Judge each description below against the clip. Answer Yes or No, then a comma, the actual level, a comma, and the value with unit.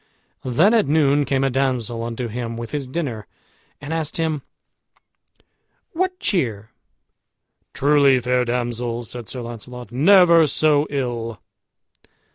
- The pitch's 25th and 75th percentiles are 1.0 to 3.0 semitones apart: No, average, 4.1 semitones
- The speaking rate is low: Yes, slow, 120 wpm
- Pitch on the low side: Yes, low, 130 Hz